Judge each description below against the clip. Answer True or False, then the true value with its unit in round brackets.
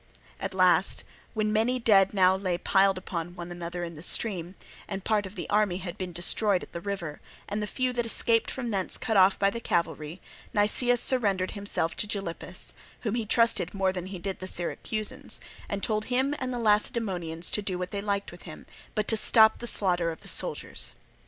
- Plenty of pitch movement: False (3.5 semitones)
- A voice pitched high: True (200 Hz)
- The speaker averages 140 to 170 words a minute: False (205 wpm)